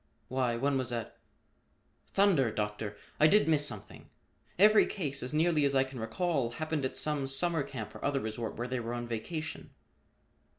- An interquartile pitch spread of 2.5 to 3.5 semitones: No, average, 4.8 semitones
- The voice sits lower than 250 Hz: Yes, low, 135 Hz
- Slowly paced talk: No, average, 175 wpm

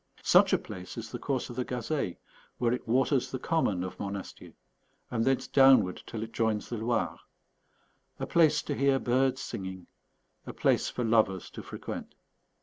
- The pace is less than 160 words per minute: No, average, 170 wpm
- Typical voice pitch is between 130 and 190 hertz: No, low, 120 Hz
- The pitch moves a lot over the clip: No, average, 3.9 semitones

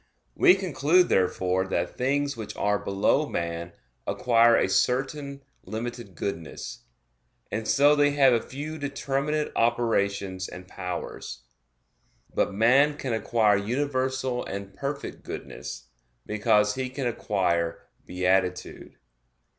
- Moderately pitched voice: No, low, 115 Hz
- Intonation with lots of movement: Yes, wide, 6.1 semitones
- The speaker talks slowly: Yes, slow, 115 wpm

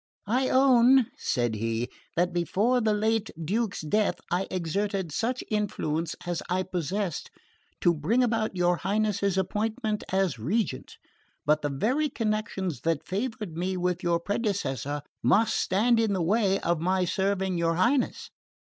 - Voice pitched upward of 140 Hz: Yes, high, 190 Hz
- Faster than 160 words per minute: No, average, 145 wpm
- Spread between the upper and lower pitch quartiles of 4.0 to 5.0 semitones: Yes, average, 4.3 semitones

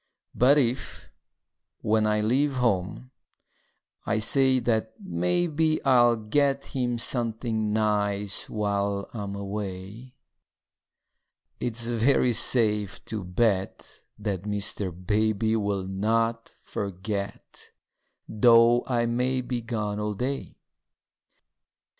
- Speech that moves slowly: Yes, slow, 95 wpm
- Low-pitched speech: Yes, low, 110 Hz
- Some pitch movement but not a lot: Yes, average, 3.1 semitones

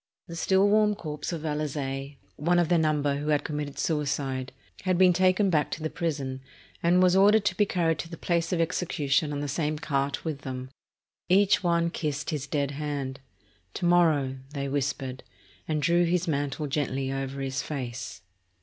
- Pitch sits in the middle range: Yes, medium, 150 Hz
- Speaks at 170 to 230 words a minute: Yes, average, 180 wpm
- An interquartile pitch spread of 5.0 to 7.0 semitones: No, average, 3.8 semitones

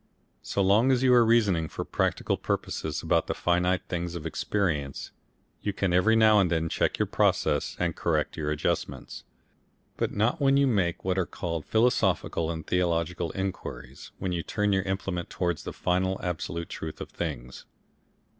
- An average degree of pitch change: Yes, average, 3.6 semitones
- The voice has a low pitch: Yes, very low, 90 Hz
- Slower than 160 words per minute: No, average, 170 wpm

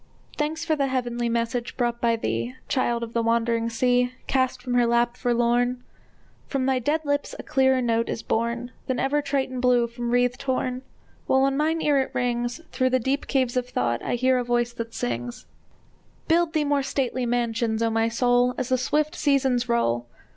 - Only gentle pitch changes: Yes, narrow, 2.1 semitones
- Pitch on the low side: No, high, 245 Hz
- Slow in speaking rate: No, average, 190 wpm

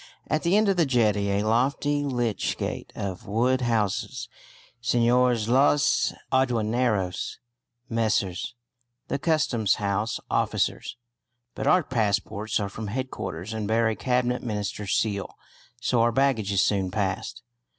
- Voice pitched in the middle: No, low, 115 Hz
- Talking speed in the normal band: No, slow, 130 wpm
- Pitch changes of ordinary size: Yes, average, 3.6 semitones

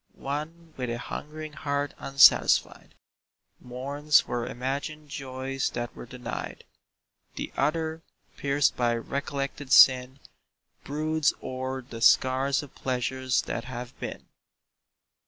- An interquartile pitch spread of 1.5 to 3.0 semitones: Yes, narrow, 2.5 semitones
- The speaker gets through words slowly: Yes, slow, 110 wpm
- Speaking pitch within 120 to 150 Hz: Yes, low, 135 Hz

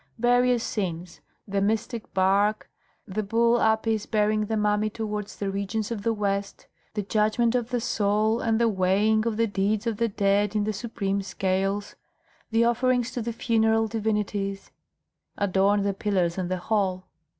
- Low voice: No, high, 210 Hz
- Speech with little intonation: Yes, narrow, 2.1 semitones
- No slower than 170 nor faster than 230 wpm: No, average, 160 wpm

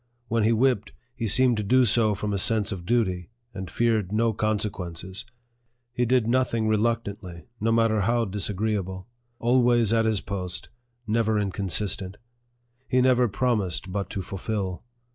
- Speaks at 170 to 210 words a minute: No, average, 145 wpm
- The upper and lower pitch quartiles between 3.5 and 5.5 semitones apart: No, average, 3.1 semitones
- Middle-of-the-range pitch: No, low, 110 Hz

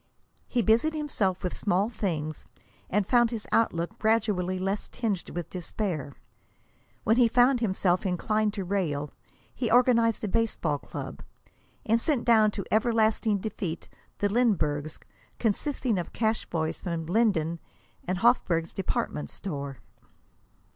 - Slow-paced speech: Yes, slow, 130 wpm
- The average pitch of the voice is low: No, high, 205 Hz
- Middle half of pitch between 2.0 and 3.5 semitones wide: No, average, 4.6 semitones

